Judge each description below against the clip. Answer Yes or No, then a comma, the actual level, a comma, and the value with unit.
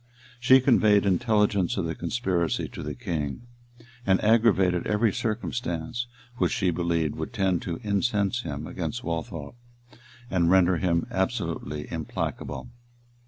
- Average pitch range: Yes, average, 4.5 semitones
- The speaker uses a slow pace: Yes, slow, 125 wpm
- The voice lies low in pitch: Yes, very low, 95 Hz